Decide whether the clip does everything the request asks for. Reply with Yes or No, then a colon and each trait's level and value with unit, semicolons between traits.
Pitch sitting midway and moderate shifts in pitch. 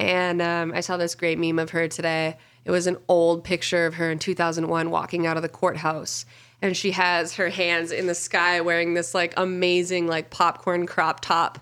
No: medium, 170 Hz; narrow, 1.4 semitones